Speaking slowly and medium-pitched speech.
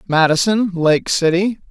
Yes: slow, 105 wpm; medium, 180 Hz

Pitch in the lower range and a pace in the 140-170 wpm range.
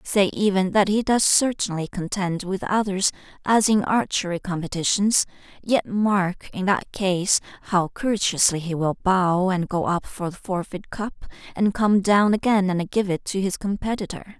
No: high, 195 Hz; average, 165 wpm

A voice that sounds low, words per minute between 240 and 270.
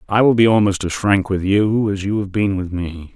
Yes: low, 100 Hz; fast, 265 wpm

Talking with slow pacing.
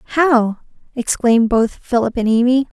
Yes: slow, 130 wpm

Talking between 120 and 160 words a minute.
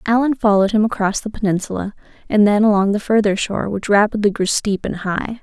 No: average, 200 wpm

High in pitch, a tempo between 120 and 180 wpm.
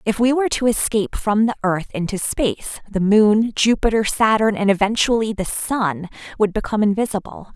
Yes: high, 210 Hz; average, 165 wpm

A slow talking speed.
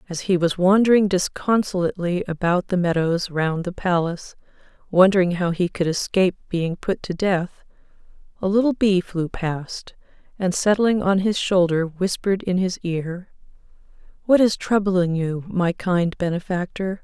No: average, 145 wpm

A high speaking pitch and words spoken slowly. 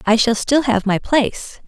No: high, 235 Hz; fast, 215 wpm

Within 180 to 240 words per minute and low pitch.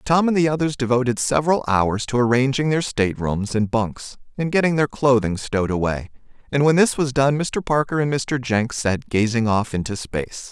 Yes: average, 195 wpm; low, 125 Hz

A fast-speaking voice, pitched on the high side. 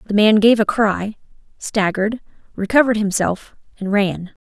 No: slow, 135 wpm; high, 210 Hz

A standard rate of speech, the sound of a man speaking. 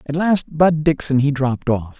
No: fast, 210 wpm; male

